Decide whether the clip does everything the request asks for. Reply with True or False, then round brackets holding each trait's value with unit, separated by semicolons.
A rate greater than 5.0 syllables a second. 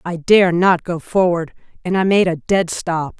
False (4.3 syllables/s)